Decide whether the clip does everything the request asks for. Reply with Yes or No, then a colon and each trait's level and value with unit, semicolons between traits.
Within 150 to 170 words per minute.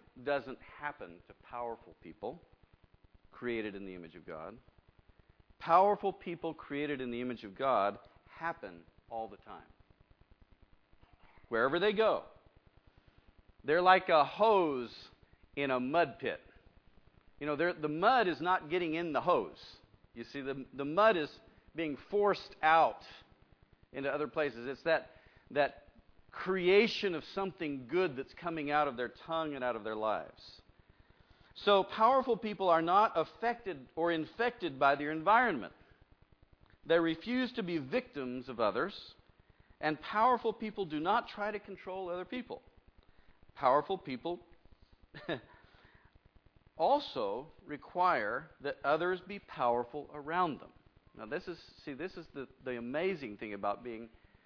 No: average, 140 wpm